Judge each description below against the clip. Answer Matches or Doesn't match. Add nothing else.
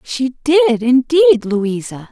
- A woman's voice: Matches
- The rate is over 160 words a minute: Doesn't match